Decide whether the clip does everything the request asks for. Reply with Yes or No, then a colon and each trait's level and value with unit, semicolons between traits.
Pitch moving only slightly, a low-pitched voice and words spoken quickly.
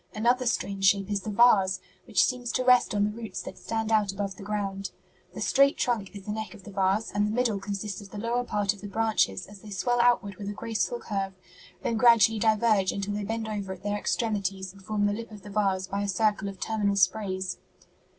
No: narrow, 2.2 semitones; high, 205 Hz; fast, 230 wpm